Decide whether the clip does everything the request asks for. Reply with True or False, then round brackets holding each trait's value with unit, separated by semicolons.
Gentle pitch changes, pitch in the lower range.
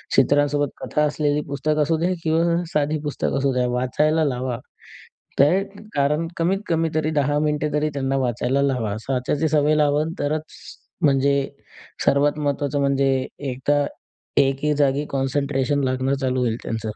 False (2.1 semitones; 145 Hz)